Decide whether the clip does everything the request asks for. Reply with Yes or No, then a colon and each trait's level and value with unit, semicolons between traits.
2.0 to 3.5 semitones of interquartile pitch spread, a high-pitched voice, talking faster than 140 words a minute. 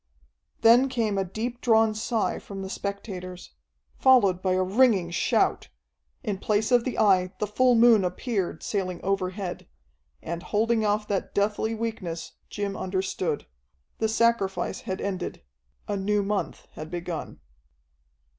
No: average, 3.1 semitones; high, 200 Hz; slow, 135 wpm